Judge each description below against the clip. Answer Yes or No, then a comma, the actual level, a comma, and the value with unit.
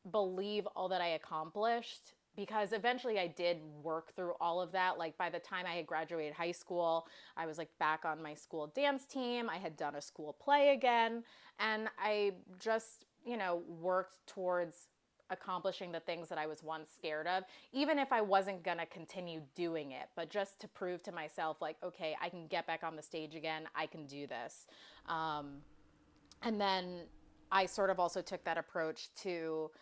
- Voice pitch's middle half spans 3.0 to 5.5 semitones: Yes, average, 3.5 semitones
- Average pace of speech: Yes, average, 190 wpm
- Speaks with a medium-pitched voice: Yes, medium, 175 Hz